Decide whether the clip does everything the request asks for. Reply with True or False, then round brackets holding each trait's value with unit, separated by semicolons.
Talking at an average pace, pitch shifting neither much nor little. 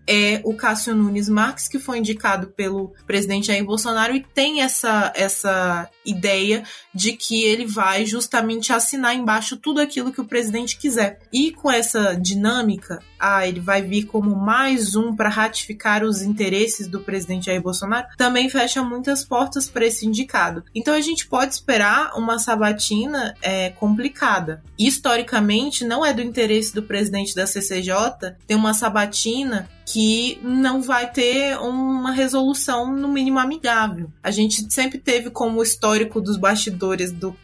True (155 wpm; 3.4 semitones)